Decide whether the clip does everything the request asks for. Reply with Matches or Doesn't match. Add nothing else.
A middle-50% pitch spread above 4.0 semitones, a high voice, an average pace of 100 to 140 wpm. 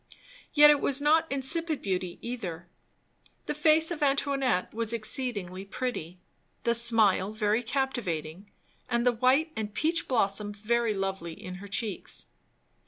Matches